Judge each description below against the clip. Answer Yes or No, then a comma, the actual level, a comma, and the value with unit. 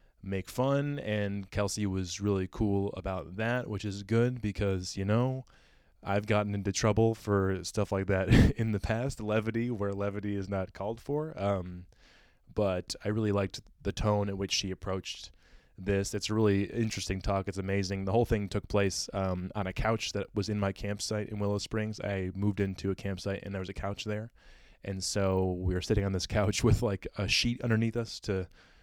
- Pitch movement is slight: Yes, narrow, 2.0 semitones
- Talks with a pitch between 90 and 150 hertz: Yes, low, 100 Hz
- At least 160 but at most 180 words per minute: No, average, 200 wpm